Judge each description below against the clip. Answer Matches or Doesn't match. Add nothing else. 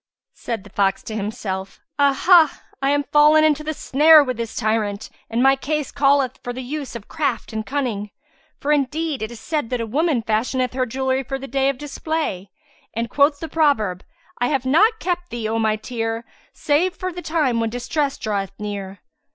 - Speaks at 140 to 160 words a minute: Doesn't match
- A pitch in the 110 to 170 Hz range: Doesn't match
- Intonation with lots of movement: Doesn't match